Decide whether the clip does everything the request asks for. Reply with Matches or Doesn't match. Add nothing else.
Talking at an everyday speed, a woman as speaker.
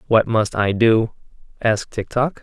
Doesn't match